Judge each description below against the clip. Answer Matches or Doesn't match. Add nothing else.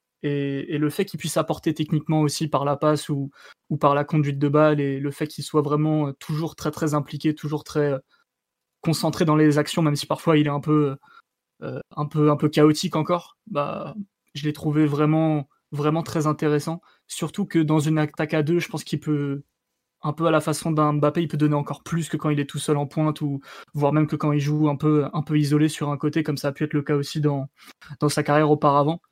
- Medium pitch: Matches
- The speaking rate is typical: Doesn't match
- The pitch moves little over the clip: Matches